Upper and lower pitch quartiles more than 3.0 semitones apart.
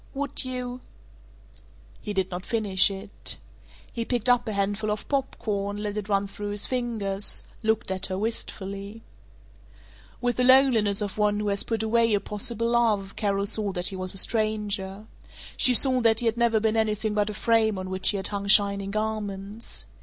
No: narrow, 2.4 semitones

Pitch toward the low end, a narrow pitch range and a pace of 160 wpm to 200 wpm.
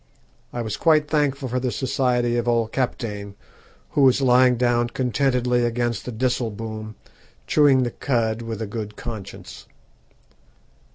No: low, 120 Hz; narrow, 2.3 semitones; slow, 135 wpm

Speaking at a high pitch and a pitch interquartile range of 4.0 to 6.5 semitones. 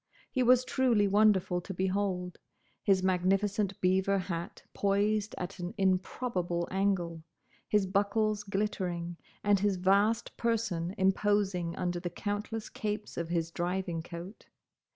No: high, 195 Hz; narrow, 2.5 semitones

